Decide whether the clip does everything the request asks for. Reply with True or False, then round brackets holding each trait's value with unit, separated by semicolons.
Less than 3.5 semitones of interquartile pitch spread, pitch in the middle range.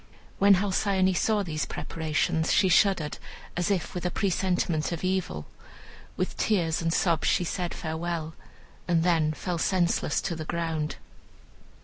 True (2.6 semitones; 175 Hz)